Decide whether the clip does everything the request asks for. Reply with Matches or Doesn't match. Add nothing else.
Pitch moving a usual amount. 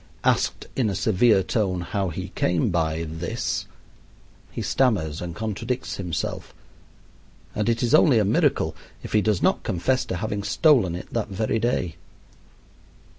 Matches